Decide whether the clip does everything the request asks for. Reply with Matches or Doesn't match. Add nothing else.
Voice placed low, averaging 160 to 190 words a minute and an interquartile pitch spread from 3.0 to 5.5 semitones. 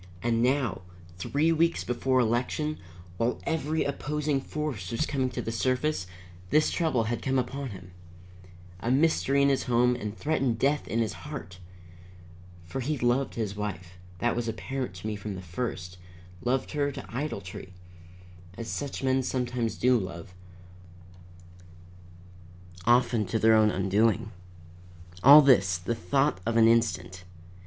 Doesn't match